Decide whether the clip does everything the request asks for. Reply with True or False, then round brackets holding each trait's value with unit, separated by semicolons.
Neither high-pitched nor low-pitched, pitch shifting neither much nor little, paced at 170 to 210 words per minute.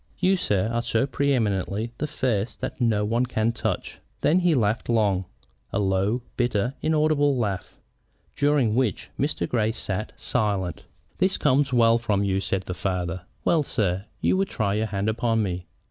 False (110 Hz; 4.6 semitones; 175 wpm)